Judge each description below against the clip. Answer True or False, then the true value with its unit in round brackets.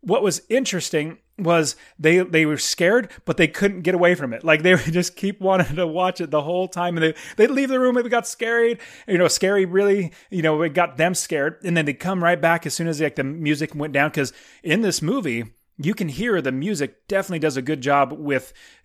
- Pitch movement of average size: True (3.8 semitones)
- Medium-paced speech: False (245 wpm)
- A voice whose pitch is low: False (175 Hz)